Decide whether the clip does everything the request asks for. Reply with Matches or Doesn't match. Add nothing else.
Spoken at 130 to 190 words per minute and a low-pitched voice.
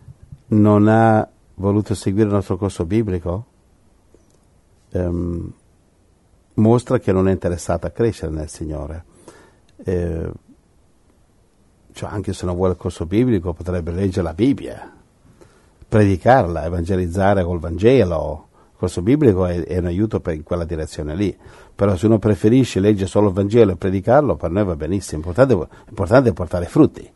Matches